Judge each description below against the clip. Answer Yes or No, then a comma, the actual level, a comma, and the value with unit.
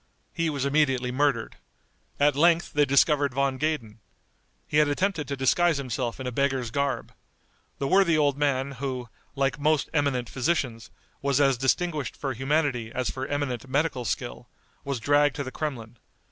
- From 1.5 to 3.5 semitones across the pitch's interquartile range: Yes, narrow, 2.4 semitones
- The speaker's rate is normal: Yes, average, 160 wpm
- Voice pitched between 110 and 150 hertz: Yes, medium, 140 Hz